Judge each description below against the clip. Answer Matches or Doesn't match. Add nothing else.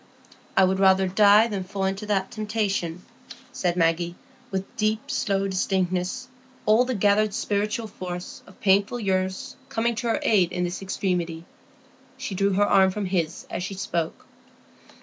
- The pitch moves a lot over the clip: Doesn't match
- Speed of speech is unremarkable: Matches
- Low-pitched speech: Doesn't match